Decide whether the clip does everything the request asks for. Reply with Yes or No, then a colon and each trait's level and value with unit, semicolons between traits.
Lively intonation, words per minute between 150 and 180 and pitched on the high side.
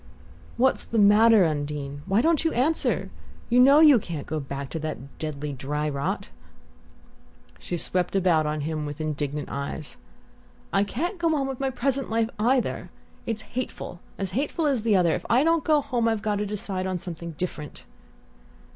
Yes: wide, 8.7 semitones; average, 175 wpm; high, 195 Hz